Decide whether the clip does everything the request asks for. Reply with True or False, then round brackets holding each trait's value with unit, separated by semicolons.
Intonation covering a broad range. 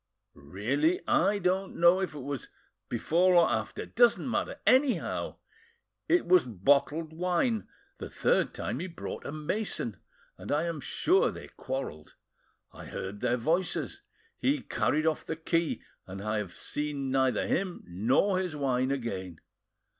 True (6.9 semitones)